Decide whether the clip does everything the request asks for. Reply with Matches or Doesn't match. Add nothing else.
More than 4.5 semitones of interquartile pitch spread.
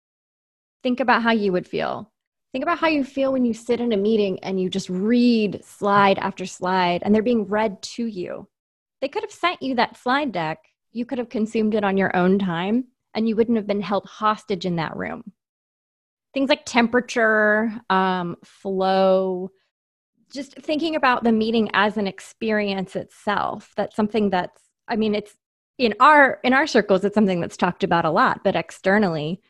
Doesn't match